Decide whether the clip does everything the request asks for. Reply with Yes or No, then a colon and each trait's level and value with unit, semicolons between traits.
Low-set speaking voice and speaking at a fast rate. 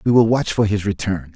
Yes: low, 100 Hz; fast, 265 wpm